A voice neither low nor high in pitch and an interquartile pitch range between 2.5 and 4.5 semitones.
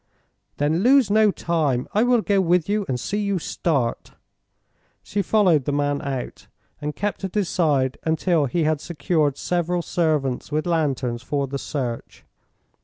No: medium, 160 Hz; average, 5.2 semitones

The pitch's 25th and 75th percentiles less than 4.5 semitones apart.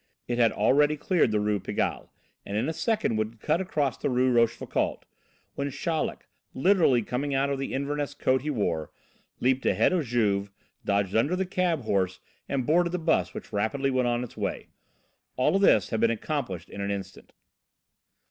No: wide, 5.5 semitones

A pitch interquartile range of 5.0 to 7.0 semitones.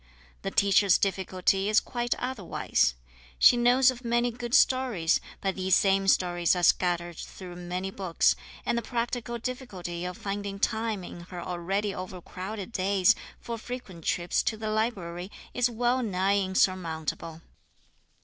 No: average, 4.6 semitones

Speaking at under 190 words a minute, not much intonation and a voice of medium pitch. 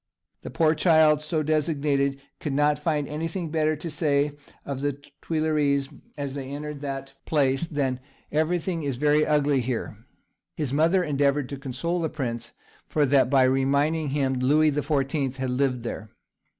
Yes: average, 160 wpm; narrow, 2.2 semitones; medium, 145 Hz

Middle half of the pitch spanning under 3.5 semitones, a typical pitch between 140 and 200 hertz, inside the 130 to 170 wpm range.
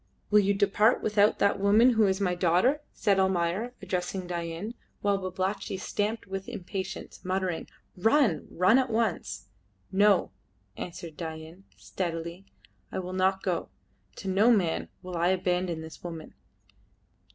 Yes: narrow, 2.6 semitones; high, 190 Hz; average, 140 wpm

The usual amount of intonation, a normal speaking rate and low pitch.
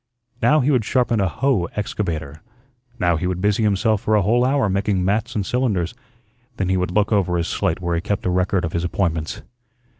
No: average, 3.6 semitones; fast, 210 wpm; low, 100 Hz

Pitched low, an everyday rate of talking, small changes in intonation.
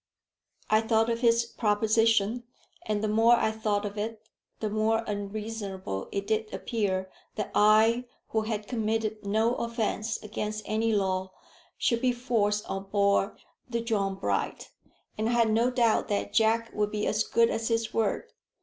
No: high, 220 Hz; average, 160 wpm; narrow, 1.6 semitones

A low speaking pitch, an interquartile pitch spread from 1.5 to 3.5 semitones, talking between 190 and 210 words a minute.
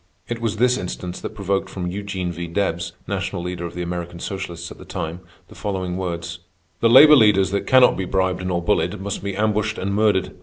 Yes: very low, 95 Hz; average, 2.9 semitones; fast, 205 wpm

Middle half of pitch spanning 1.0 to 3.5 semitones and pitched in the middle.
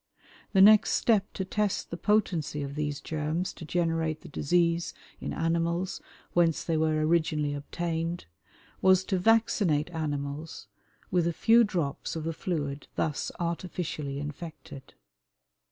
Yes: average, 2.9 semitones; medium, 165 Hz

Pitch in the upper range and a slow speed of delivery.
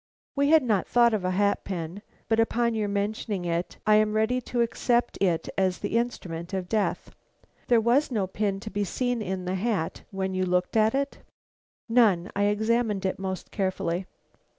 No: high, 205 Hz; average, 185 wpm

